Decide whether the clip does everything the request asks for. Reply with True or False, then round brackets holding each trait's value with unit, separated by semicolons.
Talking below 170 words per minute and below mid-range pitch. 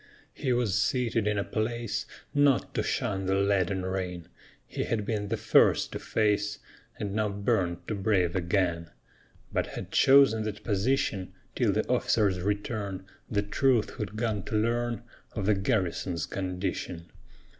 True (150 wpm; 105 Hz)